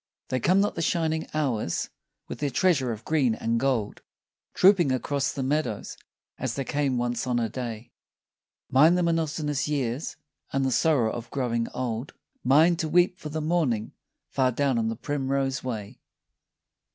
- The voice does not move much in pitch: No, average, 4.3 semitones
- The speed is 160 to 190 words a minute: Yes, average, 175 wpm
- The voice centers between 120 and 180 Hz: Yes, low, 135 Hz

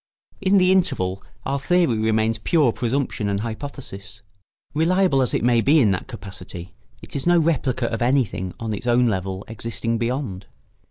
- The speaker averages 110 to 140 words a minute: No, average, 165 wpm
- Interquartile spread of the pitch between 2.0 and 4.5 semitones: No, wide, 5.6 semitones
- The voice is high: No, low, 115 Hz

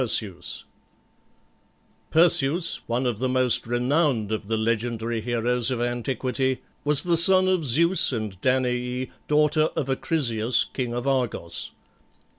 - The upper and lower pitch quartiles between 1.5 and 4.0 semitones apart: Yes, average, 3.7 semitones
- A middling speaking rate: No, slow, 125 wpm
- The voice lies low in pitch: Yes, low, 125 Hz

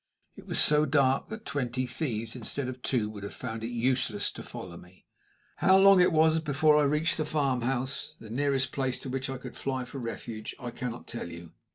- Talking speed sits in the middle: No, fast, 210 wpm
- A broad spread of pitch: No, average, 3.6 semitones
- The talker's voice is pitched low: Yes, low, 130 Hz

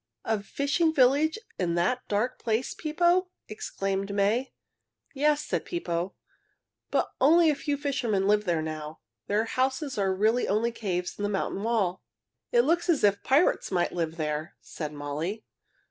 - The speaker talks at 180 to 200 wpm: No, average, 155 wpm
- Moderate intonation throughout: No, wide, 7.0 semitones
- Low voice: No, high, 215 Hz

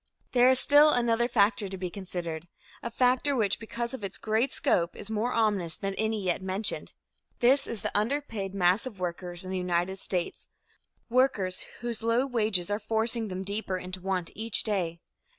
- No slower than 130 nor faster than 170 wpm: No, average, 180 wpm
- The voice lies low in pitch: No, high, 205 Hz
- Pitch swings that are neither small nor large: Yes, average, 4.1 semitones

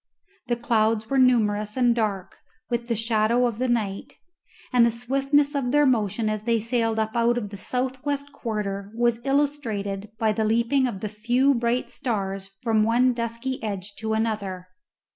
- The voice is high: Yes, high, 230 Hz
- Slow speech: No, average, 175 wpm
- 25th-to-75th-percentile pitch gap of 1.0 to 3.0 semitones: Yes, average, 2.7 semitones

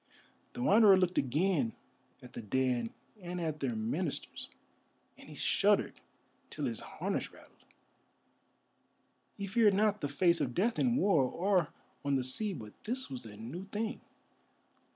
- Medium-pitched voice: Yes, medium, 175 Hz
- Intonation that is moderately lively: No, wide, 7.9 semitones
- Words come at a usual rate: Yes, average, 150 wpm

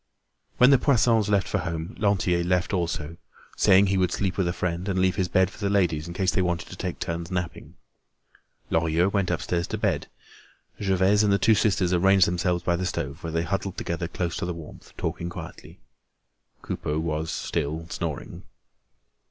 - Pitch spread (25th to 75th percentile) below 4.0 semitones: Yes, narrow, 2.5 semitones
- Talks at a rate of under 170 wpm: No, average, 185 wpm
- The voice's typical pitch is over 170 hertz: No, very low, 90 Hz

